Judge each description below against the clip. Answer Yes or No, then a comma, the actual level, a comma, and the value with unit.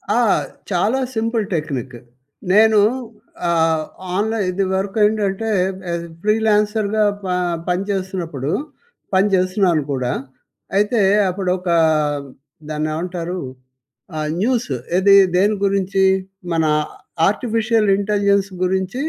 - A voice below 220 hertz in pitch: Yes, high, 195 Hz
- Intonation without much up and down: No, average, 3.3 semitones